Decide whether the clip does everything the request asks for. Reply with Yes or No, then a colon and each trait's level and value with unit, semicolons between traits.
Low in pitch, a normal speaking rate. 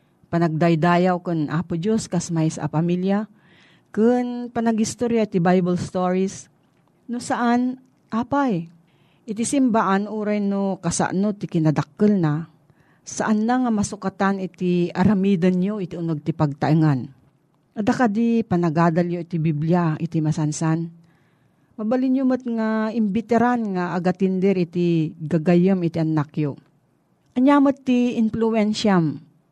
No: medium, 180 Hz; average, 120 wpm